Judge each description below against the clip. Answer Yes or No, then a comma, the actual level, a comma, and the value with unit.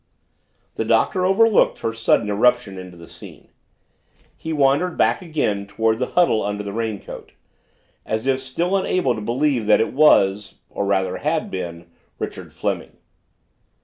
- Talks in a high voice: No, low, 115 Hz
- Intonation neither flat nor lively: No, wide, 7.0 semitones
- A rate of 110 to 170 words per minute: Yes, average, 145 wpm